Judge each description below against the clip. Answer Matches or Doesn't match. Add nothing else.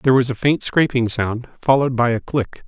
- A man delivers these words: Matches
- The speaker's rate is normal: Doesn't match